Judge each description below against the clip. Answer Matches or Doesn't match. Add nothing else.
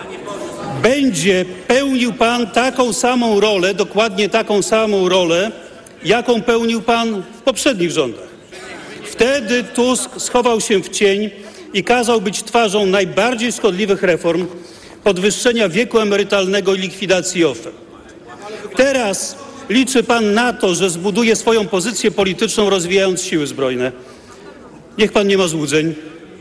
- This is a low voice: Doesn't match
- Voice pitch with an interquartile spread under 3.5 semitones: Doesn't match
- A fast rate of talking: Doesn't match